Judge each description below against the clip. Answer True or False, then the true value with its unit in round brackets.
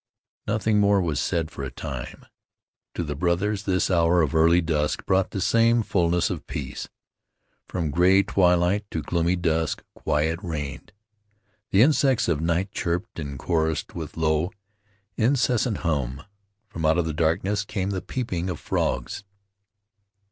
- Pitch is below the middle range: True (85 Hz)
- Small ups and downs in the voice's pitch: False (3.8 semitones)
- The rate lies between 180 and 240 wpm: False (145 wpm)